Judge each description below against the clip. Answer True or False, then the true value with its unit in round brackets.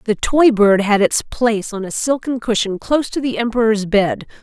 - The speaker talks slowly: False (205 wpm)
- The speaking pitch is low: False (220 Hz)